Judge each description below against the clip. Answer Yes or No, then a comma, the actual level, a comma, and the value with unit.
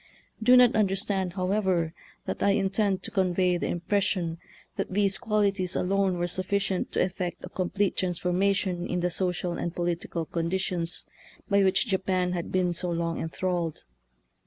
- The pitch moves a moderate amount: No, narrow, 2.1 semitones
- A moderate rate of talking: Yes, average, 160 wpm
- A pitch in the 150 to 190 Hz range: Yes, medium, 185 Hz